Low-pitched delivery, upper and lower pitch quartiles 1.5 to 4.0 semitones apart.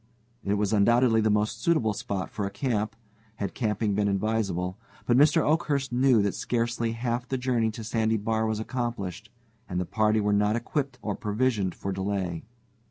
Yes: low, 110 Hz; average, 2.8 semitones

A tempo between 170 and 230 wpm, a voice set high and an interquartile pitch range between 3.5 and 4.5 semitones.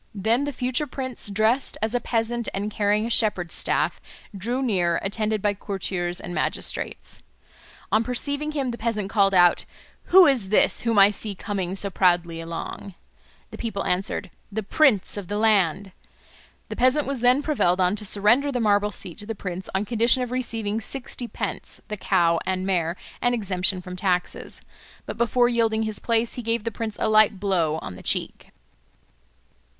Yes: average, 175 wpm; high, 210 Hz; average, 3.9 semitones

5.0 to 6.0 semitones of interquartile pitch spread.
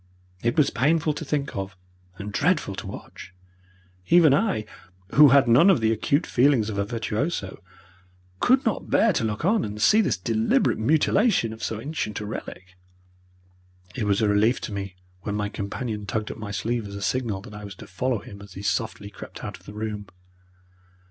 Yes: wide, 5.6 semitones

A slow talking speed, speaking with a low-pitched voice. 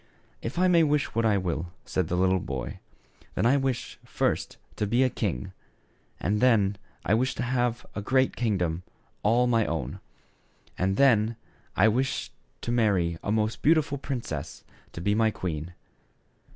No: average, 165 wpm; low, 110 Hz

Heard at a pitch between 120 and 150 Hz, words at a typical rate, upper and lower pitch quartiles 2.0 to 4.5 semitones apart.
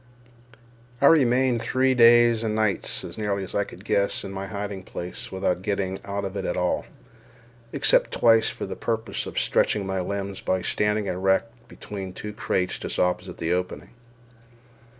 No: low, 100 Hz; average, 170 wpm; average, 2.8 semitones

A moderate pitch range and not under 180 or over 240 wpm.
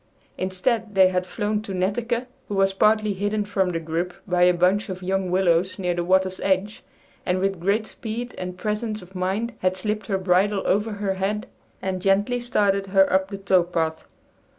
No: narrow, 2.2 semitones; average, 190 wpm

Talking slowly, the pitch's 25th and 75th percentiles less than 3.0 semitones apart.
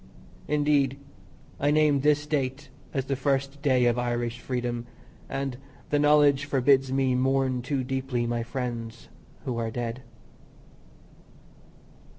Yes: slow, 125 wpm; narrow, 2.5 semitones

